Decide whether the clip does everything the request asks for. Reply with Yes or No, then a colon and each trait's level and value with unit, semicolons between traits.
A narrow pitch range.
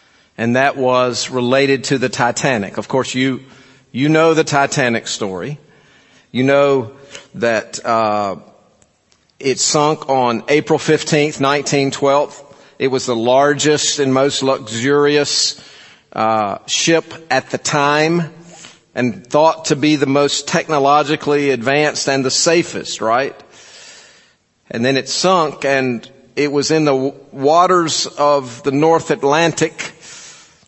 Yes: narrow, 2.3 semitones